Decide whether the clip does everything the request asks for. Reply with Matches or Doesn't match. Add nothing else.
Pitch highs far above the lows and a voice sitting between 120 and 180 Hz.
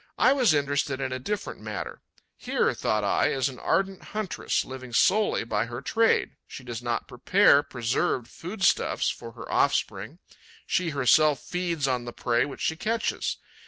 Matches